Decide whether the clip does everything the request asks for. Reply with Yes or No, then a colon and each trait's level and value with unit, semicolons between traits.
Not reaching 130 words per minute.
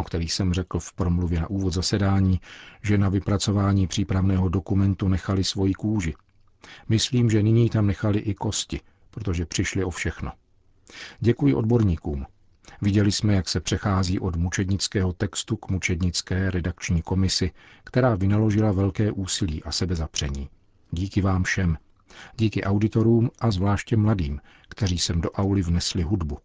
No: average, 140 wpm